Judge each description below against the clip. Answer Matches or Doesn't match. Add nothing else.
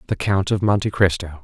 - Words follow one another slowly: Doesn't match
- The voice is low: Matches